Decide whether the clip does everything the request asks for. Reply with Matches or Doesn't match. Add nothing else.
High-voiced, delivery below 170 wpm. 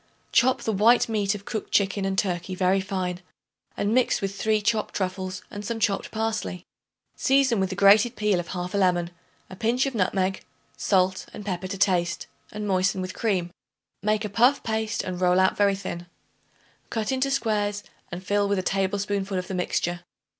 Doesn't match